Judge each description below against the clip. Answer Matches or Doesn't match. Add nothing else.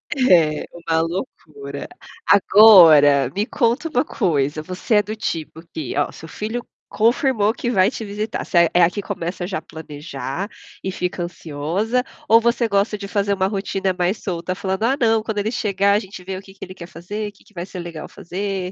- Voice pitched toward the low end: Doesn't match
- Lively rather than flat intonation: Doesn't match